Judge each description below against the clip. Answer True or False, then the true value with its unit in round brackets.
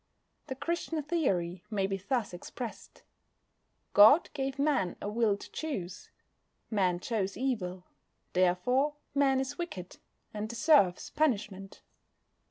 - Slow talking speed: True (115 wpm)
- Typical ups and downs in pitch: False (6.6 semitones)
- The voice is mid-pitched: False (220 Hz)